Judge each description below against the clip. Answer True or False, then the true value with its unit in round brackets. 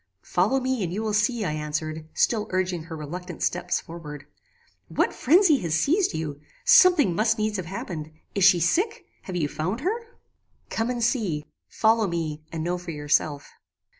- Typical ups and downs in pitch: False (6.6 semitones)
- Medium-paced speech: True (170 wpm)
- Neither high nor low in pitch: True (180 Hz)